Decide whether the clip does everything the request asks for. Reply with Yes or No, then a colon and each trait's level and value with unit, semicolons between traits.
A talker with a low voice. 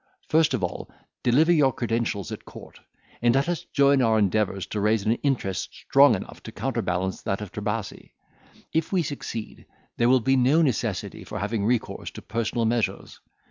Yes: low, 115 Hz